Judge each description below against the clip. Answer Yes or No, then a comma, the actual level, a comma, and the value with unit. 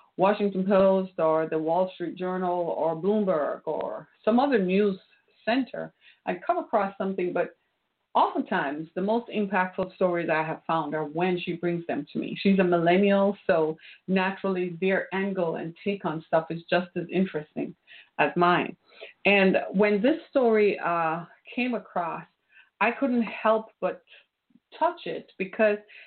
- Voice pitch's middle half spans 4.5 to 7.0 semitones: No, average, 3.3 semitones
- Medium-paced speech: Yes, average, 150 wpm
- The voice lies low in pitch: No, high, 190 Hz